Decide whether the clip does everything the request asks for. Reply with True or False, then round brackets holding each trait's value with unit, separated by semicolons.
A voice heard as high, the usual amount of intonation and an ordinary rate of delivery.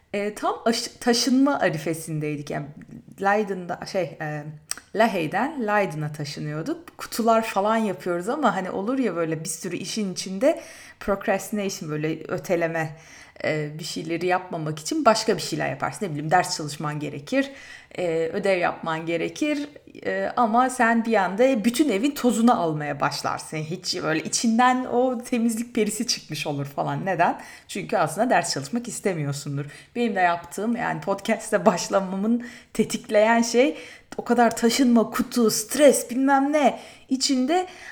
False (210 Hz; 6.3 semitones; 130 wpm)